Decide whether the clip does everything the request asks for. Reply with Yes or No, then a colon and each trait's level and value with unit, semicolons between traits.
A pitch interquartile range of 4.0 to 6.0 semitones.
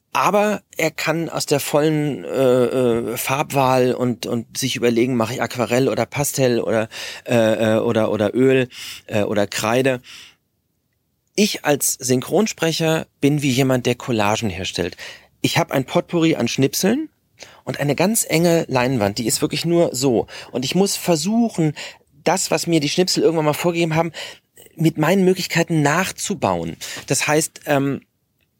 Yes: average, 5.0 semitones